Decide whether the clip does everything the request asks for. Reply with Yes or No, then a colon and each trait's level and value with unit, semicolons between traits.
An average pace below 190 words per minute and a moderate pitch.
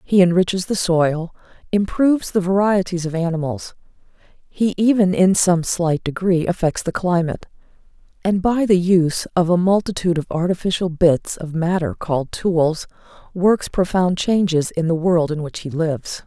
Yes: average, 155 wpm; medium, 175 Hz